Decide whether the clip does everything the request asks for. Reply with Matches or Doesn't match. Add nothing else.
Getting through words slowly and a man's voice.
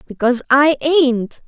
Doesn't match